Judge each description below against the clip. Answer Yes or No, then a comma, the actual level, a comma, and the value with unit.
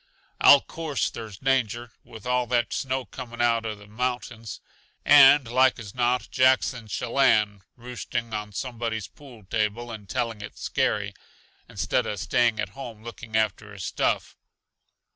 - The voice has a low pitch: Yes, low, 115 Hz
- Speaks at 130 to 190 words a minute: Yes, average, 150 wpm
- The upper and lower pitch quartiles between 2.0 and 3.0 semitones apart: Yes, average, 2.7 semitones